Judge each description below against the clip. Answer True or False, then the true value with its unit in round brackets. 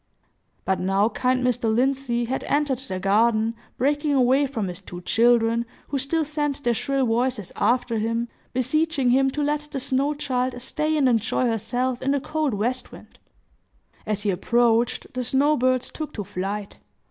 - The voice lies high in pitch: True (250 Hz)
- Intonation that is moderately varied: True (3.4 semitones)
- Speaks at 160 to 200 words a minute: True (170 wpm)